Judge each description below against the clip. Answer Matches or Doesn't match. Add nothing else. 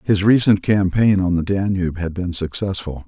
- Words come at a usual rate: Matches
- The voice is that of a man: Matches